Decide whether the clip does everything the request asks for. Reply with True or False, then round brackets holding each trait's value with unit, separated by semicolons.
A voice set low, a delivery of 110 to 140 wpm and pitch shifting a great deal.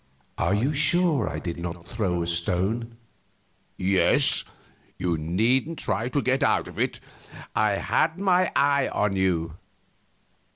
True (105 Hz; 135 wpm; 8.0 semitones)